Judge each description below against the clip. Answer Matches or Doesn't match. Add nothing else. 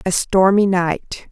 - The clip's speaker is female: Matches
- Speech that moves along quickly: Doesn't match